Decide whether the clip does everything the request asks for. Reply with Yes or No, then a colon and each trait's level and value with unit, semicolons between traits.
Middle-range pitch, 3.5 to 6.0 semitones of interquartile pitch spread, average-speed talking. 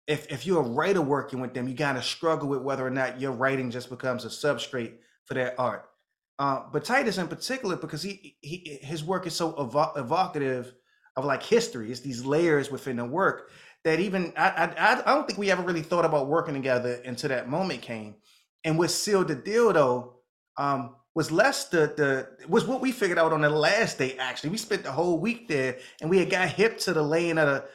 No: medium, 150 Hz; average, 5.0 semitones; fast, 220 wpm